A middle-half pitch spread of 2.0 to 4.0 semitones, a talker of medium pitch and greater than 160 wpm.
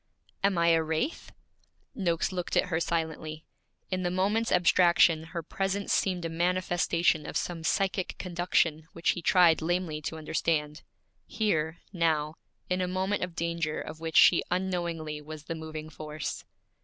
No: narrow, 2.4 semitones; medium, 170 Hz; average, 155 wpm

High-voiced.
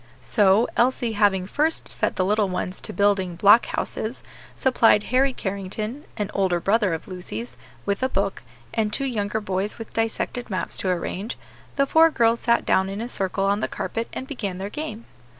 Yes: high, 210 Hz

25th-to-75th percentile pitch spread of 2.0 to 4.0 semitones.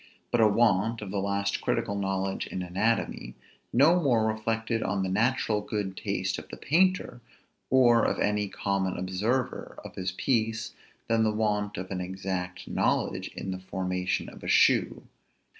Yes: average, 3.2 semitones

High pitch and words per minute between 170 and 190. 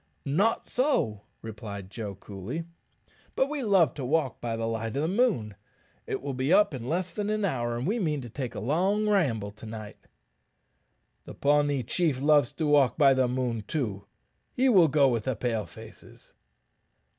No: low, 135 Hz; average, 180 wpm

